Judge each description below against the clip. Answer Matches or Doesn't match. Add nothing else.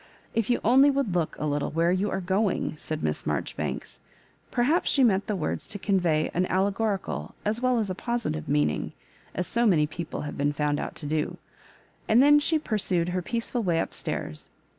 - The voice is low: Doesn't match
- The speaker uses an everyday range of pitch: Doesn't match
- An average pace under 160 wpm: Doesn't match